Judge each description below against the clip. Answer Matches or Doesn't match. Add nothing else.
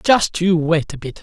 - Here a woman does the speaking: Doesn't match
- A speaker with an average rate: Doesn't match